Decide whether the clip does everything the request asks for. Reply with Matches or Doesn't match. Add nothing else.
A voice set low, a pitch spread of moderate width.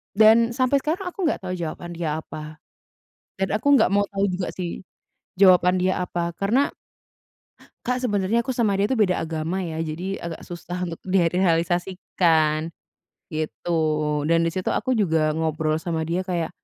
Doesn't match